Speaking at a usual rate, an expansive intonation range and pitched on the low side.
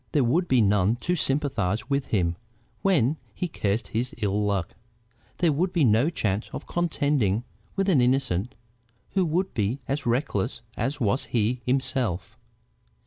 Yes: average, 150 wpm; wide, 5.9 semitones; low, 125 Hz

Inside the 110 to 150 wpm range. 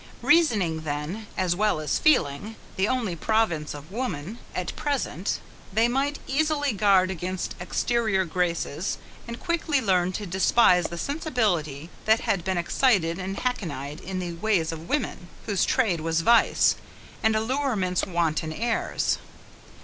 Yes: average, 140 wpm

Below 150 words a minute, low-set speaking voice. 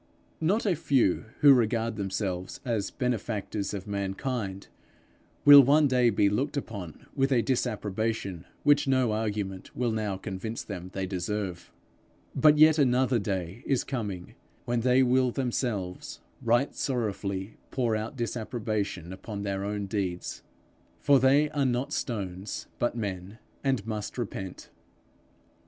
Yes: slow, 135 wpm; low, 110 Hz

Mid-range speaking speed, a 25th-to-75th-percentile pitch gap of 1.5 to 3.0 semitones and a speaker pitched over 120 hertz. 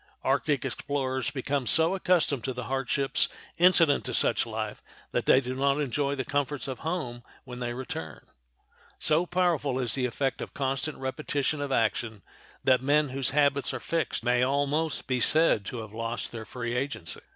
Yes: average, 175 wpm; average, 2.7 semitones; low, 135 Hz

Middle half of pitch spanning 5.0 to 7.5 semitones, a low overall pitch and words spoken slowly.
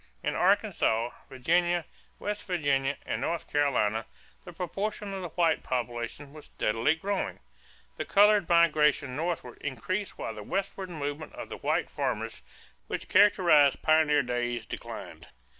No: wide, 5.5 semitones; medium, 155 Hz; slow, 130 wpm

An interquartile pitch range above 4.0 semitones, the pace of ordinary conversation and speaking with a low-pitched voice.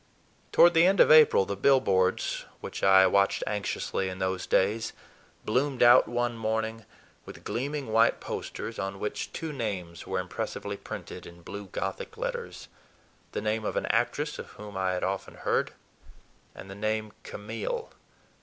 Yes: average, 4.5 semitones; average, 155 wpm; low, 105 Hz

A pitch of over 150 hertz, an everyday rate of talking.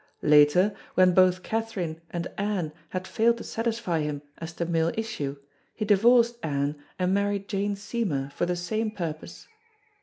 Yes: medium, 185 Hz; average, 155 wpm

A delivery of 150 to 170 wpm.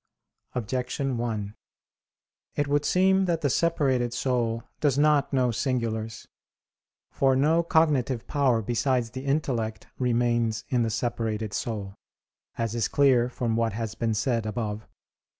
No: slow, 135 wpm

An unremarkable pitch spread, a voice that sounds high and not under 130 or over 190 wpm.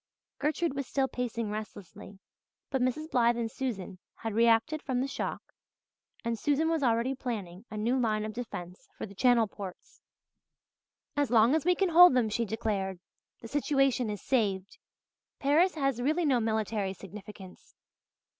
Yes: average, 4.4 semitones; high, 235 Hz; average, 155 wpm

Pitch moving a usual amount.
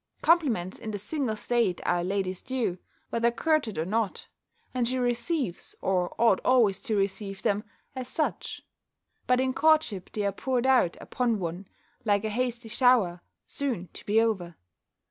Yes: average, 4.7 semitones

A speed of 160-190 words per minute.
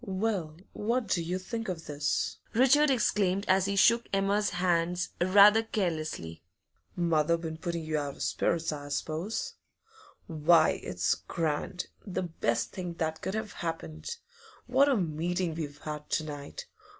No: average, 150 wpm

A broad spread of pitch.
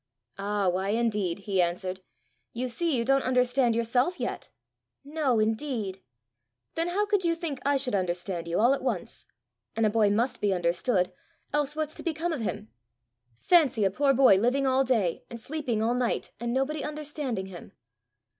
Yes: wide, 5.8 semitones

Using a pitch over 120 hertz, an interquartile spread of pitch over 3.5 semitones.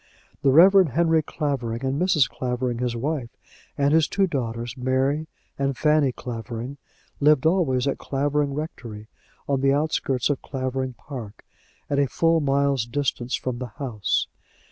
No: low, 135 Hz; average, 3.2 semitones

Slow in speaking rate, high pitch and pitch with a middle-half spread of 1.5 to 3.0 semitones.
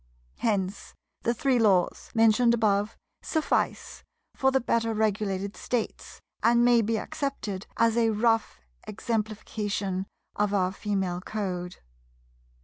Yes: slow, 115 wpm; high, 215 Hz; average, 2.7 semitones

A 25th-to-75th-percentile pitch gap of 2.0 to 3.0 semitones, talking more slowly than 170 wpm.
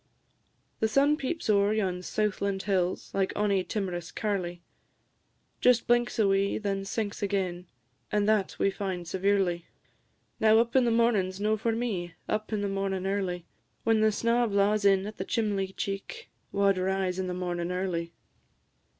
Yes: narrow, 2.5 semitones; average, 160 wpm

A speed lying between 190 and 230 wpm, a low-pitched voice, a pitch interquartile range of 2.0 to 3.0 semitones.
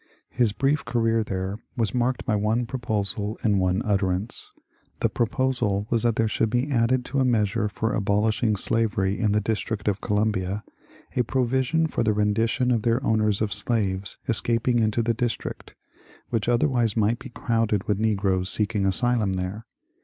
No: average, 170 wpm; low, 110 Hz; narrow, 2.6 semitones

